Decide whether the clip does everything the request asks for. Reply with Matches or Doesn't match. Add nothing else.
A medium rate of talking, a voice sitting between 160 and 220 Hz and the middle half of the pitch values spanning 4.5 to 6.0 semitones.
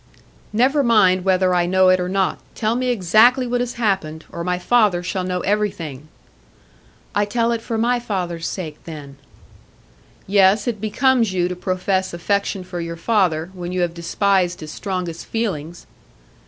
Doesn't match